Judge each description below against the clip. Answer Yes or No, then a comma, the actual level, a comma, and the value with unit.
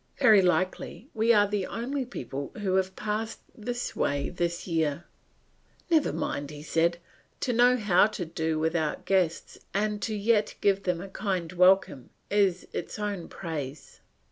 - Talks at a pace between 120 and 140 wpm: No, average, 155 wpm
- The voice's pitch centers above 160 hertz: Yes, high, 190 Hz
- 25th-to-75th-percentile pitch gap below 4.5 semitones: Yes, average, 4.0 semitones